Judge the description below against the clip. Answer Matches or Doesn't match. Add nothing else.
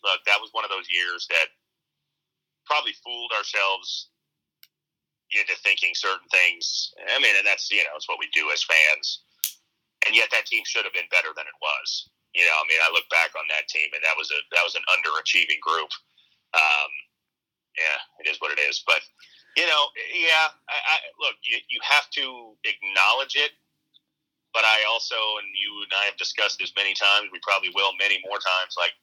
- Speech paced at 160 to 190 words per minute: Doesn't match